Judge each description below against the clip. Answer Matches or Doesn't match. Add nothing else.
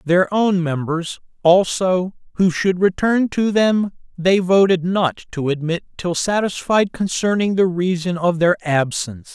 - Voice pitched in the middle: Matches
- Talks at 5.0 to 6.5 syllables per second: Doesn't match